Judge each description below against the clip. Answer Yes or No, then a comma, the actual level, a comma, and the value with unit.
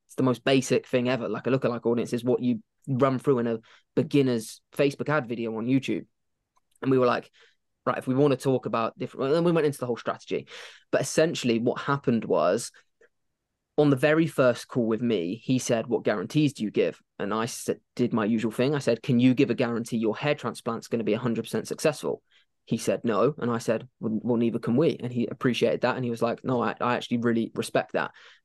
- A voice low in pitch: Yes, low, 120 Hz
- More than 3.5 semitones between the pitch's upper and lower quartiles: No, narrow, 2.4 semitones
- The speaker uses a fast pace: Yes, fast, 230 wpm